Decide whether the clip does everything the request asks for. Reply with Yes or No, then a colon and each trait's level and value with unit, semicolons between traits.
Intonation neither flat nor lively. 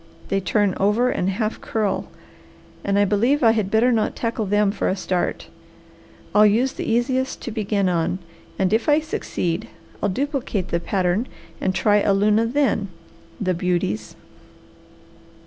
Yes: average, 3.3 semitones